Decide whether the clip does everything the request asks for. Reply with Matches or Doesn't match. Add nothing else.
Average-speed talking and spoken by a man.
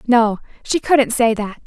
Doesn't match